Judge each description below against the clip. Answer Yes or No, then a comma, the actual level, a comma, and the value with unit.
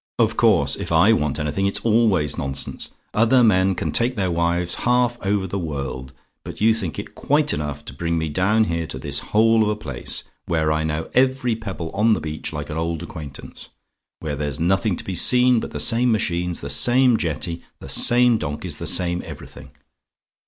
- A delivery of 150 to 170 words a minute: No, average, 195 wpm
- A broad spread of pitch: Yes, wide, 6.5 semitones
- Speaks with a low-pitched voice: Yes, very low, 90 Hz